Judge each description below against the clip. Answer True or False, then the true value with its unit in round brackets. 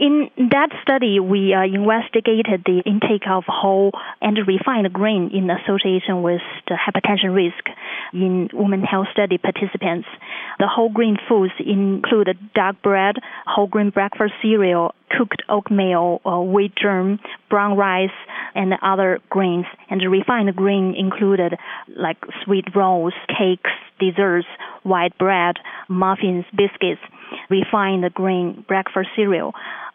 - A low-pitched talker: False (195 Hz)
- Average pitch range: False (1.8 semitones)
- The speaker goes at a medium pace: False (120 wpm)